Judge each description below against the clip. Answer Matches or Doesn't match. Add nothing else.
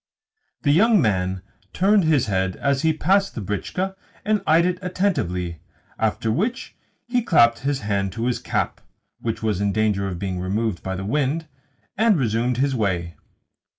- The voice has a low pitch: Matches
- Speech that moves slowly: Doesn't match